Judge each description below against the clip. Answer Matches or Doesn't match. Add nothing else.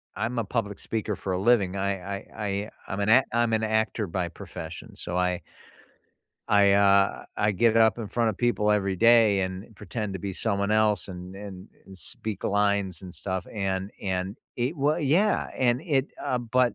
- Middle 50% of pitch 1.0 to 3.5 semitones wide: Matches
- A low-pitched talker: Matches